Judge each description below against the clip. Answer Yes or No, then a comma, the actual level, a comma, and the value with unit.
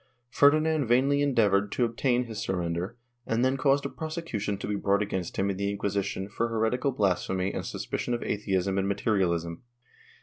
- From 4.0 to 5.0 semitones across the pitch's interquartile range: Yes, average, 4.3 semitones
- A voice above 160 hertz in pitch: No, low, 105 Hz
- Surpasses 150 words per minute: Yes, average, 170 wpm